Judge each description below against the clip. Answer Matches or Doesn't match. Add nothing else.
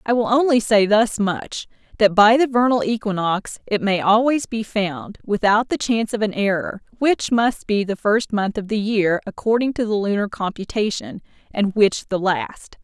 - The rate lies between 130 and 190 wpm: Matches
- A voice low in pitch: Doesn't match